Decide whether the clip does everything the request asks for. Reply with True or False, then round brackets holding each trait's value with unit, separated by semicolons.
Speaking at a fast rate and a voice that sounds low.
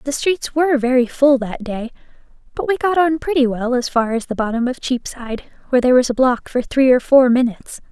False (225 wpm; 260 Hz)